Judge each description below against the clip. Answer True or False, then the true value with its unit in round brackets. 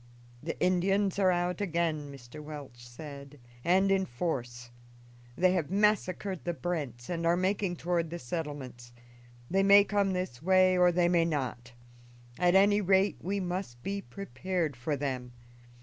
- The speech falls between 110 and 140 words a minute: False (150 wpm)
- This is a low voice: False (175 Hz)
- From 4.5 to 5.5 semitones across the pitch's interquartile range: True (4.9 semitones)